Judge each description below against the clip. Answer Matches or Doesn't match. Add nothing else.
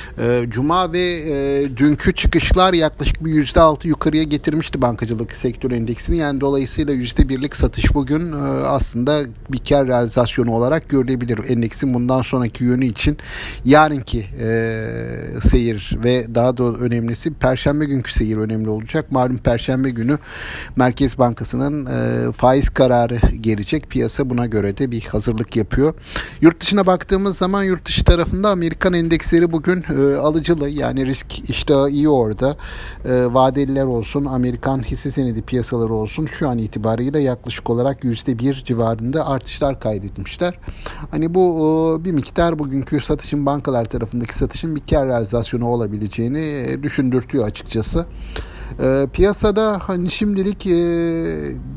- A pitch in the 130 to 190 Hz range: Matches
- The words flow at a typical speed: Matches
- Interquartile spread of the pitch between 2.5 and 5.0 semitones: Matches